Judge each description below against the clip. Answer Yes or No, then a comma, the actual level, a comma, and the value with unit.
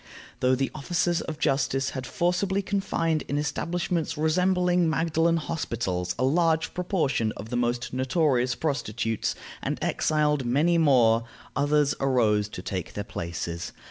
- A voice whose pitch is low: No, medium, 145 Hz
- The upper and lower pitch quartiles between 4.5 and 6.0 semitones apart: Yes, wide, 5.4 semitones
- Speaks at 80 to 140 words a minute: Yes, slow, 135 wpm